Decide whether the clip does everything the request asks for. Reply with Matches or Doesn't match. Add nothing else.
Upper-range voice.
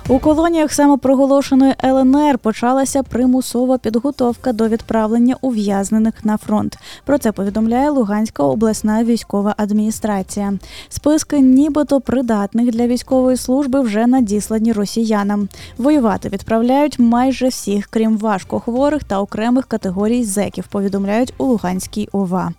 Matches